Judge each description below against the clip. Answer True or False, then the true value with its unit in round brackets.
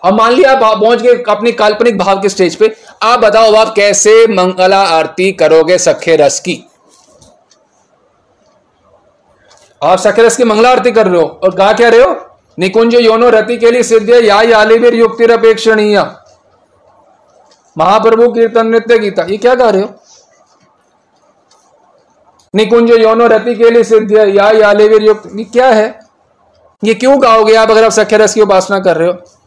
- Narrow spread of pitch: True (2.2 semitones)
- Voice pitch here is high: True (220 Hz)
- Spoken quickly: False (145 wpm)